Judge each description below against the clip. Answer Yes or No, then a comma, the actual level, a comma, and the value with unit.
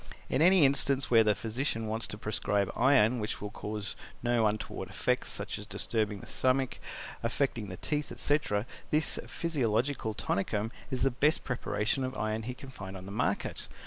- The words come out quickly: No, average, 175 wpm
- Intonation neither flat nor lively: Yes, average, 4.3 semitones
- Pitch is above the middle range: No, low, 115 Hz